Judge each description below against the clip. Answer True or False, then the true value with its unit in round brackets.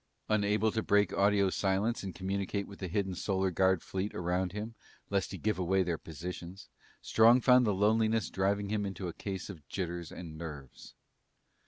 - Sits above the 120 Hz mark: False (95 Hz)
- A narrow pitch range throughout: True (2.3 semitones)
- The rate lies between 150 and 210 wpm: True (175 wpm)